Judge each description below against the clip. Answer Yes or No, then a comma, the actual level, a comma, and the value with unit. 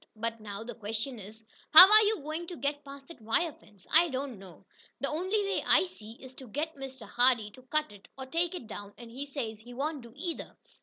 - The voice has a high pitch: Yes, very high, 265 Hz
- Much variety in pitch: Yes, wide, 5.8 semitones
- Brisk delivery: Yes, fast, 235 wpm